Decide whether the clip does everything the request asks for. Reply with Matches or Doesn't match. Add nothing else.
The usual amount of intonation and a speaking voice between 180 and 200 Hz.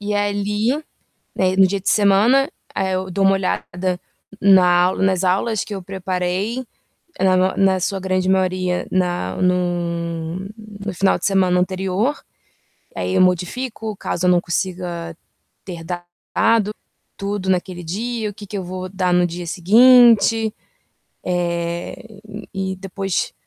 Doesn't match